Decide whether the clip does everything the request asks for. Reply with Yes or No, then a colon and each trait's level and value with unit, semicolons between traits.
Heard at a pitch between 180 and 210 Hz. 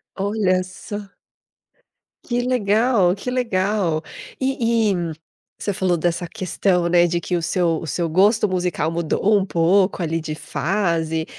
Yes: medium, 185 Hz